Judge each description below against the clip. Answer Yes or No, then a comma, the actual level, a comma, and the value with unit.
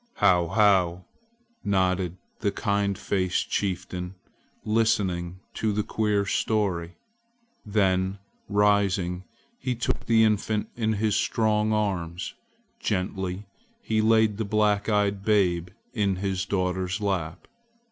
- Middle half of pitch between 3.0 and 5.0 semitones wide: No, narrow, 2.5 semitones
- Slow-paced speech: Yes, slow, 110 wpm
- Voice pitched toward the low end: Yes, low, 100 Hz